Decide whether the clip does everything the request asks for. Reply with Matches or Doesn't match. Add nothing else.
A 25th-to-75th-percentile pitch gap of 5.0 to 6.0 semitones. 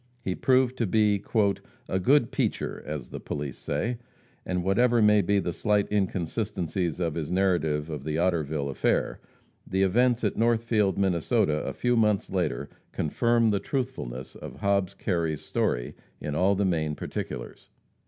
Matches